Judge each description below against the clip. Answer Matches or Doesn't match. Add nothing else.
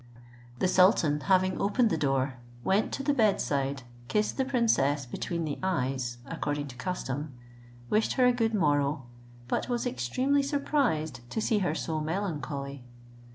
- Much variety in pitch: Matches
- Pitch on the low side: Doesn't match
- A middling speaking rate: Matches